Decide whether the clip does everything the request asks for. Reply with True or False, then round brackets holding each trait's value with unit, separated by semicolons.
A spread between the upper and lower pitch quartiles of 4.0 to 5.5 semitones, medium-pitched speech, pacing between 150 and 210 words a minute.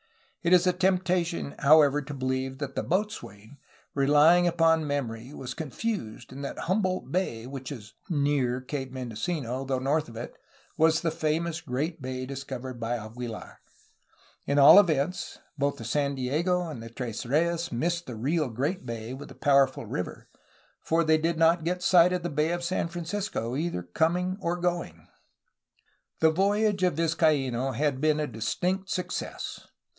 True (4.9 semitones; 150 Hz; 165 wpm)